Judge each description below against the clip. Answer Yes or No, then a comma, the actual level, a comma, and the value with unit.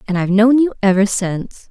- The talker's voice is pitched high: Yes, high, 210 Hz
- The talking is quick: Yes, fast, 210 wpm